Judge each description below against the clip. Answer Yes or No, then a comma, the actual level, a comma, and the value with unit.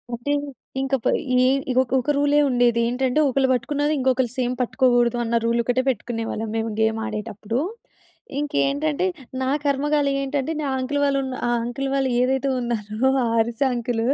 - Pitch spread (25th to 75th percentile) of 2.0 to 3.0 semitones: Yes, average, 2.7 semitones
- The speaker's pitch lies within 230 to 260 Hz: Yes, very high, 250 Hz